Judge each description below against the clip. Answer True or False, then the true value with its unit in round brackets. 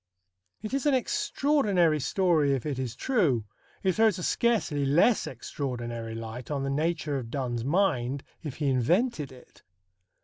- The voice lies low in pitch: False (145 Hz)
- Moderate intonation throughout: False (7.5 semitones)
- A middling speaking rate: True (150 wpm)